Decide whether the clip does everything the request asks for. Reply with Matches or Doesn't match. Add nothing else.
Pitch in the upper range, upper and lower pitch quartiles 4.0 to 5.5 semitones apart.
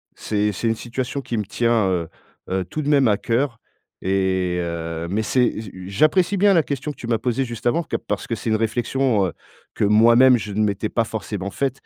Doesn't match